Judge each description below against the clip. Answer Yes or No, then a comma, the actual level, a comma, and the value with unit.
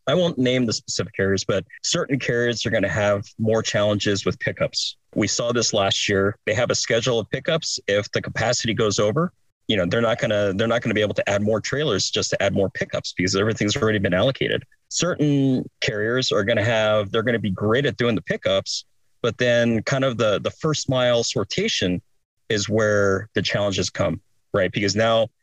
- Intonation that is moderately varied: Yes, average, 3.0 semitones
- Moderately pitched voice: No, low, 110 Hz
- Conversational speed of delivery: No, fast, 215 wpm